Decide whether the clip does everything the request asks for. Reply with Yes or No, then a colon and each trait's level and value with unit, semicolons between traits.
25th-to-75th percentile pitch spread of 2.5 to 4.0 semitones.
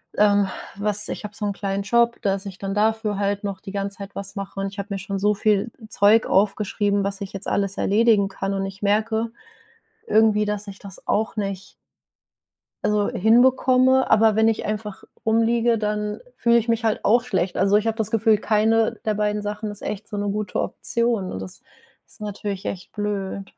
No: narrow, 1.8 semitones